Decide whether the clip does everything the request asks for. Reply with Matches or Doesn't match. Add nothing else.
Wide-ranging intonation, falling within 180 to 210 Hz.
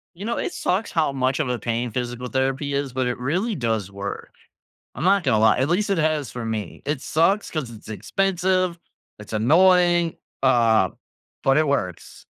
Doesn't match